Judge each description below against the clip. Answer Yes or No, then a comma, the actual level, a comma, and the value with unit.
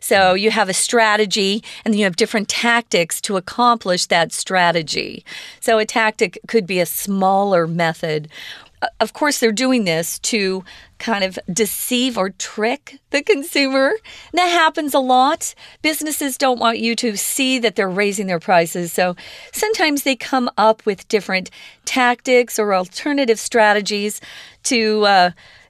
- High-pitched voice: Yes, high, 220 Hz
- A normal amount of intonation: Yes, average, 5.0 semitones